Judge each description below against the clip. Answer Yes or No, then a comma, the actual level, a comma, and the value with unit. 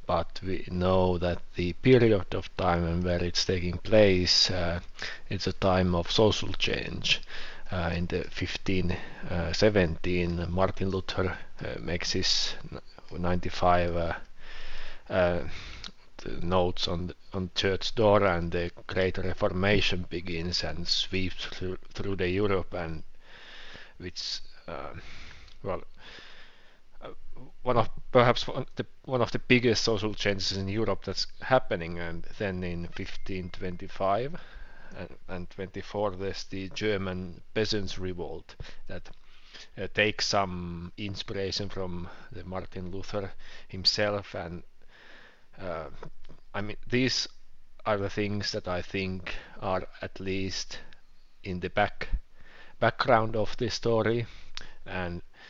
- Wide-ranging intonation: No, narrow, 2.6 semitones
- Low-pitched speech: Yes, very low, 95 Hz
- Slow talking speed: Yes, slow, 125 wpm